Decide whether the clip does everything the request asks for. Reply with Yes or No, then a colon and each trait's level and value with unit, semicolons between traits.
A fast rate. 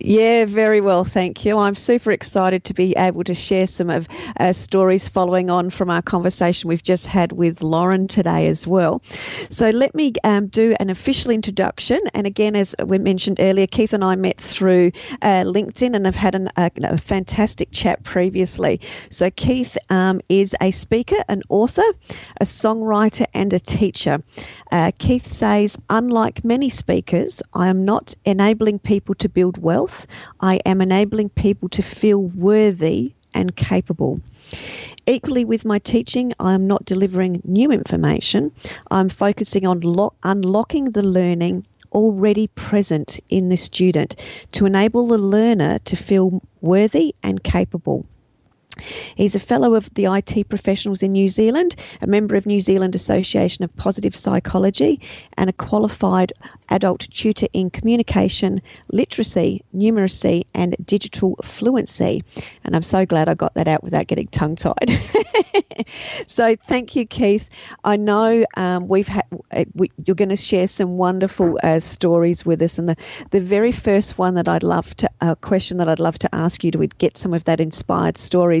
No: average, 165 wpm